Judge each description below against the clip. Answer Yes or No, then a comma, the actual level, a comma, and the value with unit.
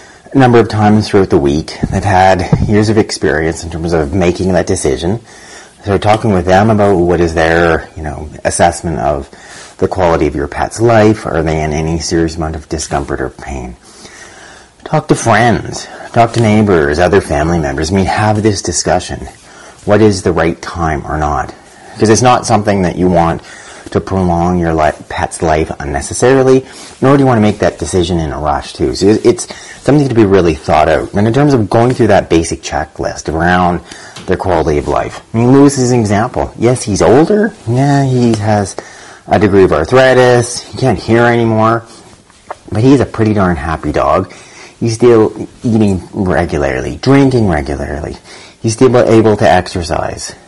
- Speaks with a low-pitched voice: Yes, low, 100 Hz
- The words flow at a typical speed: Yes, average, 185 wpm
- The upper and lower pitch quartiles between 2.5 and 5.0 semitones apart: No, wide, 5.6 semitones